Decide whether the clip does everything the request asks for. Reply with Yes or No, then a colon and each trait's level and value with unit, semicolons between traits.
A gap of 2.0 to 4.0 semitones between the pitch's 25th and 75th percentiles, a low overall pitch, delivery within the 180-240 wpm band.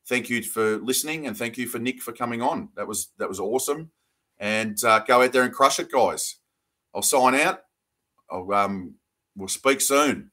Yes: average, 3.3 semitones; low, 120 Hz; average, 200 wpm